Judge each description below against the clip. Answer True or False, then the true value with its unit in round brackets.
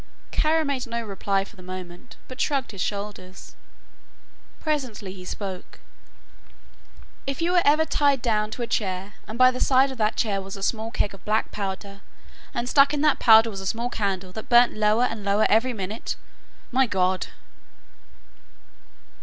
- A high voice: True (220 Hz)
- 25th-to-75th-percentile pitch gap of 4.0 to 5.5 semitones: True (4.5 semitones)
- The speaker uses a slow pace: False (170 wpm)